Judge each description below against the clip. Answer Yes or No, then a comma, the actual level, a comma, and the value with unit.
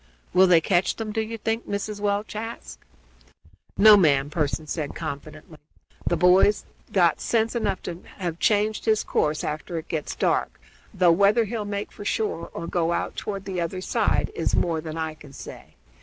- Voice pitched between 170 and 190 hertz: Yes, medium, 185 Hz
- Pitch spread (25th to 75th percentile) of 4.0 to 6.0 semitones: Yes, average, 4.4 semitones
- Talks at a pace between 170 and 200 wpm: Yes, average, 180 wpm